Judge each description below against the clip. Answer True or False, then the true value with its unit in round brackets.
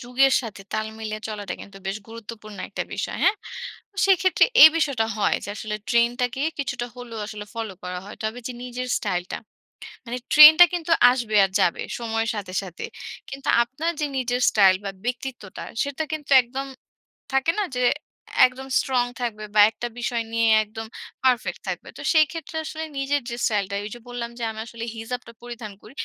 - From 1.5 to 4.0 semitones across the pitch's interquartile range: True (3.5 semitones)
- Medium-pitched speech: False (240 Hz)